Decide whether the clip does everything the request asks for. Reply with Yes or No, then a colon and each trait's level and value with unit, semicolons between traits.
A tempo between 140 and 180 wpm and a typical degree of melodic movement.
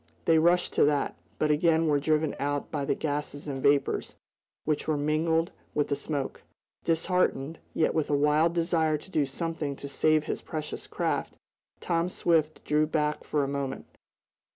No: average, 170 wpm; narrow, 2.0 semitones